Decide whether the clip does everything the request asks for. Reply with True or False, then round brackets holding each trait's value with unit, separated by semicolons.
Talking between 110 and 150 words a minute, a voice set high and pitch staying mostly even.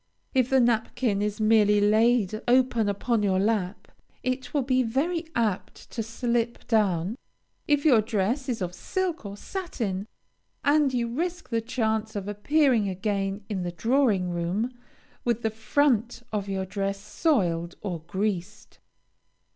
False (145 wpm; 220 Hz; 4.1 semitones)